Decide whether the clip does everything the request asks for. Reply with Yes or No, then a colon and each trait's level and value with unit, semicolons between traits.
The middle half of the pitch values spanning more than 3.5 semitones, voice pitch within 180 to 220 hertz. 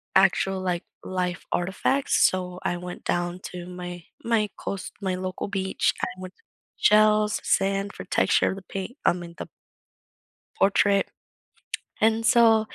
No: average, 2.7 semitones; high, 190 Hz